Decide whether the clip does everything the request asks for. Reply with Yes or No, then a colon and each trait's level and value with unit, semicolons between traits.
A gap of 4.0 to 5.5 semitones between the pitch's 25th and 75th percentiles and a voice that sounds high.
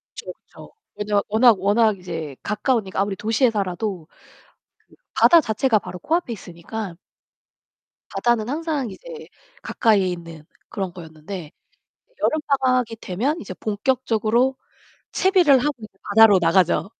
Yes: average, 5.2 semitones; high, 215 Hz